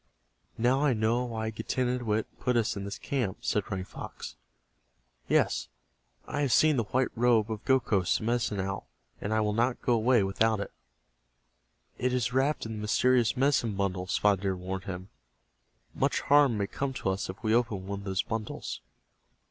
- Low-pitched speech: Yes, low, 110 Hz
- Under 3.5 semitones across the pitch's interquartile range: No, average, 3.9 semitones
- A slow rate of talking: No, average, 180 wpm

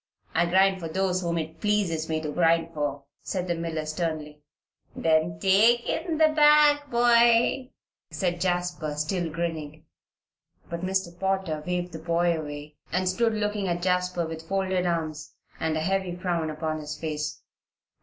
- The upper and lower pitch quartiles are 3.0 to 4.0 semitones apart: Yes, average, 3.3 semitones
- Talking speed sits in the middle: Yes, average, 155 wpm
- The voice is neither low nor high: Yes, medium, 175 Hz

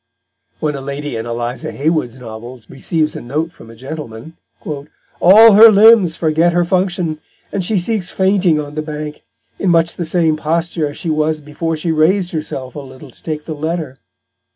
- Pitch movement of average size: Yes, average, 3.3 semitones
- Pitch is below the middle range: No, medium, 155 Hz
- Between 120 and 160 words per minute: No, average, 180 wpm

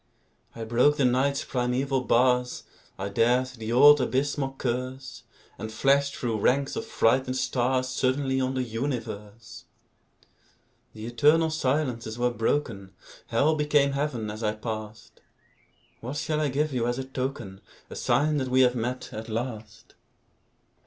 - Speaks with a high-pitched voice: No, low, 130 Hz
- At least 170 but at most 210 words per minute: No, average, 145 wpm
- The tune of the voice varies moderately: Yes, average, 3.3 semitones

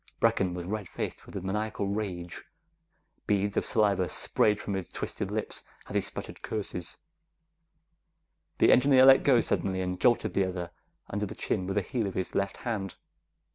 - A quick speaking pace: No, average, 175 wpm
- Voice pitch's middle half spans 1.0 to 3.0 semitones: Yes, narrow, 2.5 semitones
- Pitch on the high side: No, low, 100 Hz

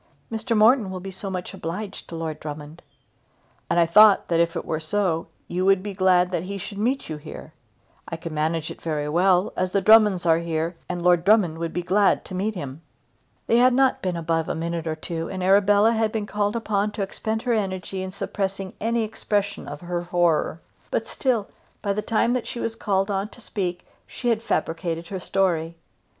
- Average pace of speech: No, fast, 210 wpm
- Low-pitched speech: No, high, 190 Hz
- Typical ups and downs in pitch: Yes, average, 3.8 semitones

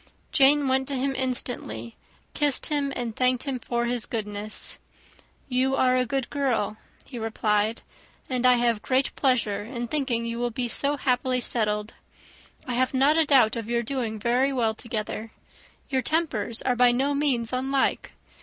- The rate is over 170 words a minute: No, average, 165 wpm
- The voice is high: Yes, very high, 250 Hz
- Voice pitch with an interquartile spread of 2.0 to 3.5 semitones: Yes, average, 2.8 semitones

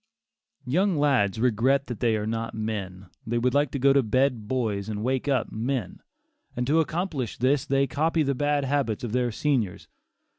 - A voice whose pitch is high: No, low, 125 Hz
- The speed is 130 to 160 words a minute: No, average, 185 wpm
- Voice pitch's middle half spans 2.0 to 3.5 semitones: No, average, 4.1 semitones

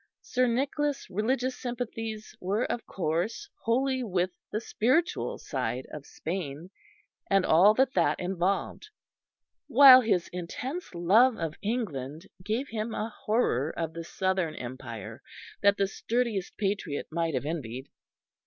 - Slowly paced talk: Yes, slow, 130 wpm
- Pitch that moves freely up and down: Yes, wide, 6.3 semitones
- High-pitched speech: Yes, high, 200 Hz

